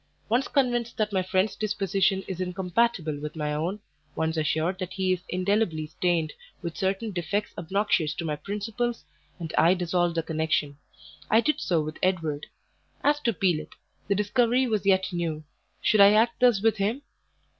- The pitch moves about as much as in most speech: Yes, average, 4.4 semitones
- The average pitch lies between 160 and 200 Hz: Yes, high, 190 Hz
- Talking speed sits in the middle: Yes, average, 165 wpm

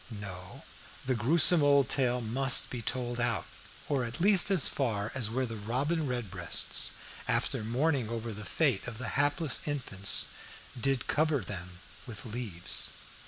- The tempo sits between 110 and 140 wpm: No, average, 150 wpm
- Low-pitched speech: Yes, low, 120 Hz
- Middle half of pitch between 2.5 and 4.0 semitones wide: No, average, 4.5 semitones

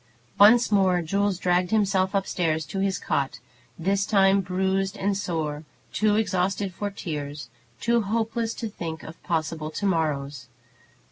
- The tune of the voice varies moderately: Yes, average, 3.9 semitones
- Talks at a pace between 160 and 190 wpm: No, average, 145 wpm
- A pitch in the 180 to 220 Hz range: Yes, high, 190 Hz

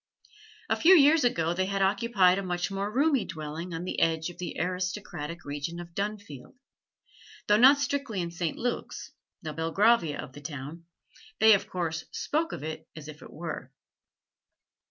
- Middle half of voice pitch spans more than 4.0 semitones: Yes, average, 4.6 semitones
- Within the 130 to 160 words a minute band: No, average, 170 wpm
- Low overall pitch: No, medium, 180 Hz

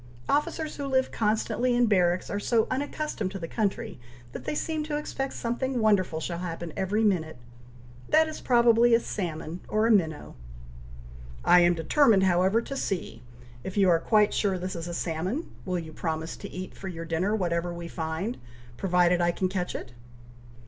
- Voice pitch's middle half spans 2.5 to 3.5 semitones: No, average, 5.2 semitones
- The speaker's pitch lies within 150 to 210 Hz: Yes, high, 190 Hz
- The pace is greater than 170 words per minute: Yes, average, 180 wpm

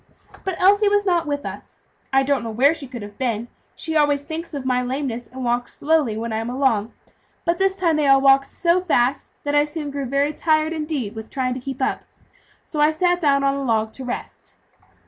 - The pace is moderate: No, fast, 225 wpm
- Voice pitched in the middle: No, very high, 275 Hz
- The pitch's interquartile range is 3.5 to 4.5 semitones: Yes, average, 4.1 semitones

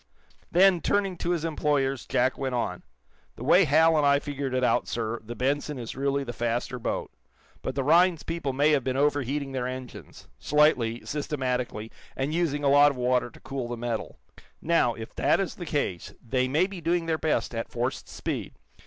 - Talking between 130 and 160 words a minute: No, average, 195 wpm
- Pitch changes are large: No, average, 3.6 semitones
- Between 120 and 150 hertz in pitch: Yes, medium, 140 Hz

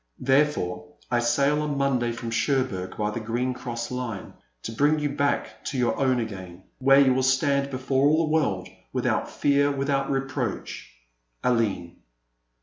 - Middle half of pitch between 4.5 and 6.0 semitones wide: No, average, 3.2 semitones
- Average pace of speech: Yes, average, 160 wpm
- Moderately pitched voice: No, low, 130 Hz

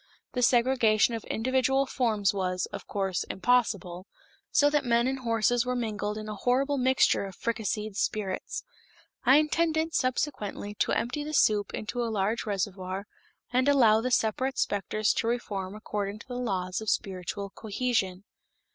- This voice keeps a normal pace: Yes, average, 155 wpm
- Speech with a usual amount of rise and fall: Yes, average, 4.0 semitones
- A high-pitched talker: Yes, high, 220 Hz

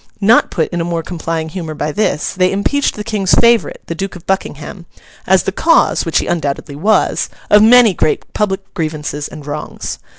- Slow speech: No, average, 190 wpm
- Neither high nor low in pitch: Yes, medium, 180 Hz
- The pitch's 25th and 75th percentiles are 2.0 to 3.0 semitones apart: No, average, 4.6 semitones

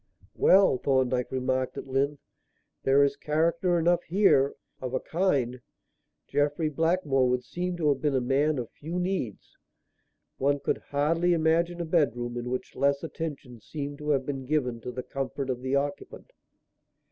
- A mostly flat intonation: No, average, 3.9 semitones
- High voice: No, medium, 140 Hz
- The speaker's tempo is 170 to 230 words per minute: No, average, 160 wpm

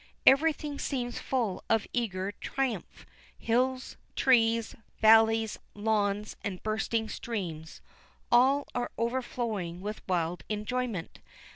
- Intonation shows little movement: No, average, 3.4 semitones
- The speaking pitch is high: Yes, high, 225 Hz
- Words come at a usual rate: No, slow, 105 wpm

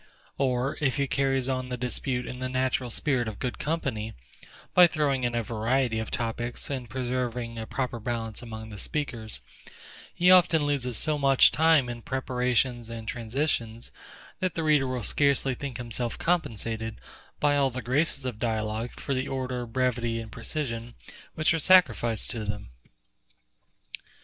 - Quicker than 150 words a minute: Yes, average, 160 wpm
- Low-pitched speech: Yes, low, 125 Hz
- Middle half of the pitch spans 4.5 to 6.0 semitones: No, average, 3.0 semitones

